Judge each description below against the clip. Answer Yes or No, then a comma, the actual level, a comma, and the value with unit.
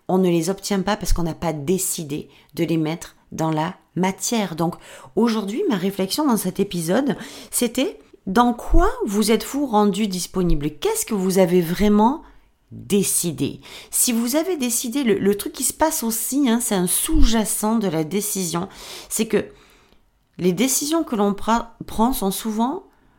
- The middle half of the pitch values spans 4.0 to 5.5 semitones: Yes, average, 4.4 semitones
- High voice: Yes, high, 205 Hz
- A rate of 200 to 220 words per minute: No, average, 165 wpm